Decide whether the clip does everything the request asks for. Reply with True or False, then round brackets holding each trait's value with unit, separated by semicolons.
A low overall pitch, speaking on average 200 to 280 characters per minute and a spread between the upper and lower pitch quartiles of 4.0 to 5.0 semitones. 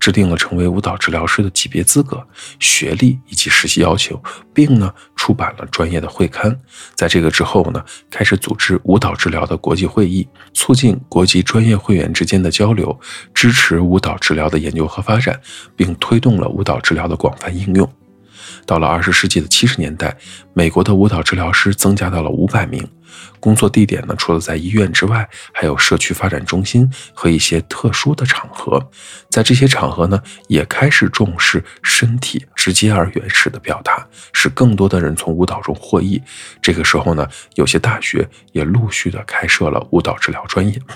False (95 Hz; 290 characters per minute; 4.5 semitones)